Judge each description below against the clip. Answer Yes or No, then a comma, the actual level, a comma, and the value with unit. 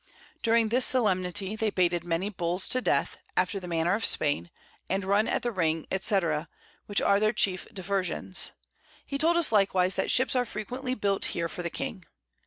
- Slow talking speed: No, average, 185 wpm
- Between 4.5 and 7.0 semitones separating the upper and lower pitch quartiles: No, average, 3.7 semitones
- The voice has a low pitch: No, high, 195 Hz